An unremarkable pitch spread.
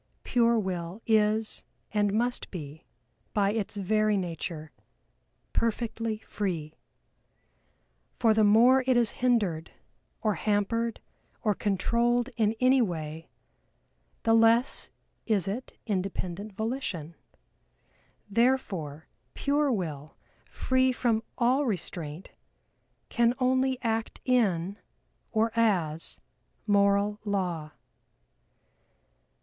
Yes: average, 4.3 semitones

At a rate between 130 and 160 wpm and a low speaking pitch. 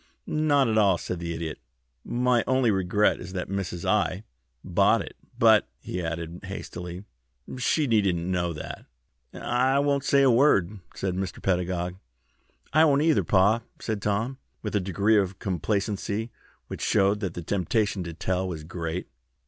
Yes: average, 155 wpm; low, 100 Hz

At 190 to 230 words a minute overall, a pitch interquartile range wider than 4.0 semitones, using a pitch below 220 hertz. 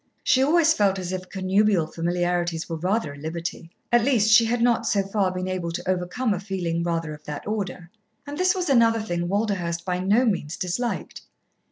Yes: average, 195 wpm; average, 4.6 semitones; medium, 185 Hz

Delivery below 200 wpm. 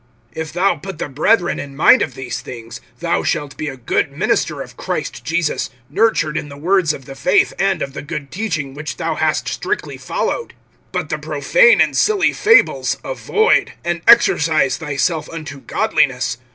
Yes: average, 175 wpm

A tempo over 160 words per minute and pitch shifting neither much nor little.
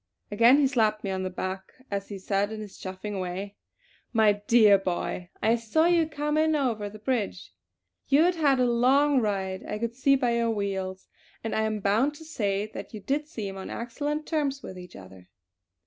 No: average, 200 wpm; wide, 5.7 semitones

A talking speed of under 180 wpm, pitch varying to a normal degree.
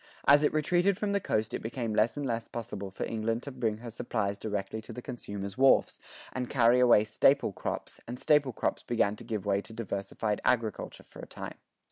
No: fast, 205 wpm; average, 3.3 semitones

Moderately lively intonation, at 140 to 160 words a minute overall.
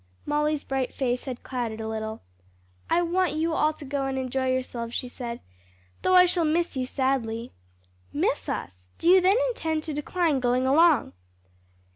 No: average, 4.6 semitones; average, 170 wpm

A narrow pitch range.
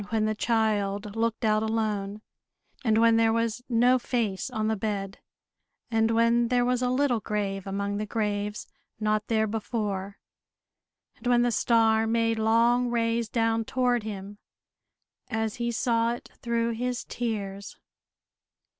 Yes: narrow, 1.9 semitones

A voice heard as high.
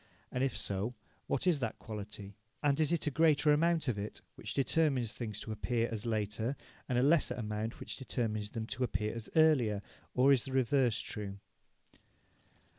No: low, 120 Hz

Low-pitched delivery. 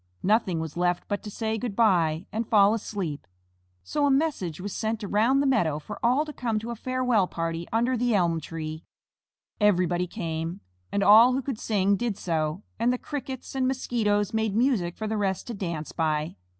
No: high, 205 Hz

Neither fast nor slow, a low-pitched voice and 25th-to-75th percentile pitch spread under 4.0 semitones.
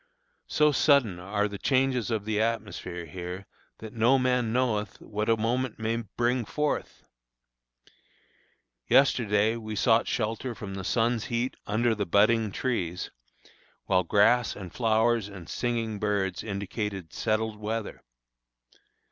No: slow, 130 wpm; low, 110 Hz; narrow, 2.6 semitones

